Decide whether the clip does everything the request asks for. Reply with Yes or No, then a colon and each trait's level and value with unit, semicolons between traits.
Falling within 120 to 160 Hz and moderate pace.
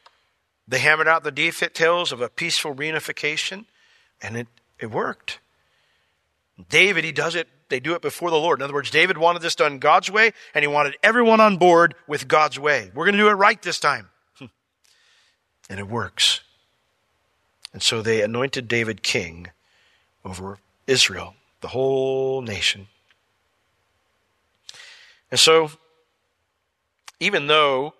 Yes: low, 135 Hz; average, 145 wpm